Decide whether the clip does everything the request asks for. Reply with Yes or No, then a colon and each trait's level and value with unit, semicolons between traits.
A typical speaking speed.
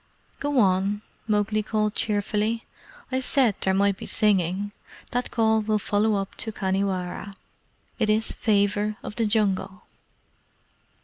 No: slow, 130 wpm